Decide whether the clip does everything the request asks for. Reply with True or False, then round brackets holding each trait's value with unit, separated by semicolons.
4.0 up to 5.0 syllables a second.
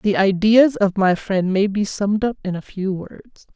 True (4.4 syllables/s)